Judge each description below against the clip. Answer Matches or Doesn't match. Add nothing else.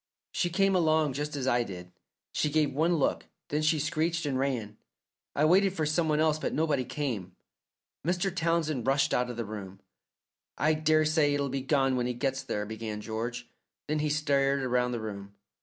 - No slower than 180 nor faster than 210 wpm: Matches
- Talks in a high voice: Doesn't match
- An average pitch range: Matches